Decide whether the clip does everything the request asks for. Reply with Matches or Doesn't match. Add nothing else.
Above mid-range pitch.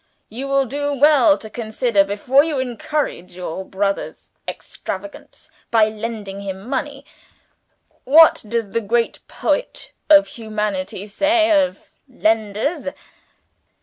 Matches